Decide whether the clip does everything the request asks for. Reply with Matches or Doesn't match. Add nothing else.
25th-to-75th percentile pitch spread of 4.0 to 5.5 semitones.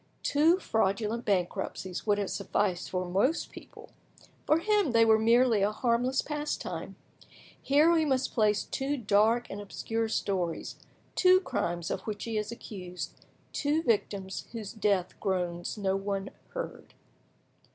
Matches